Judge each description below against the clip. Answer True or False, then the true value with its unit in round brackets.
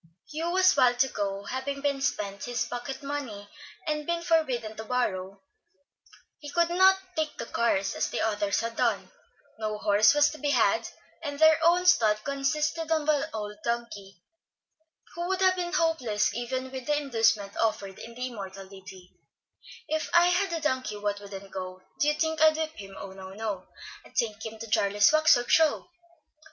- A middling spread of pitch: False (7.0 semitones)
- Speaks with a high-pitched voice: True (245 Hz)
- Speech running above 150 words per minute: True (185 wpm)